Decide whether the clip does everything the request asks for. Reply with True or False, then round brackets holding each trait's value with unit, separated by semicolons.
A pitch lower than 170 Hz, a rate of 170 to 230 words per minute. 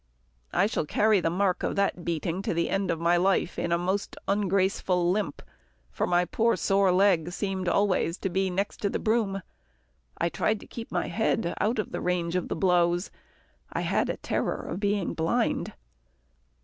False (185 Hz; 180 wpm)